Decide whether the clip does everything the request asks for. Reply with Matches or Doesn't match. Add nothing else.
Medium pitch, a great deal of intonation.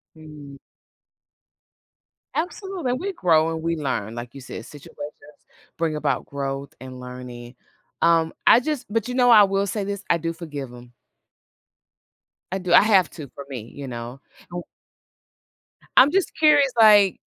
Matches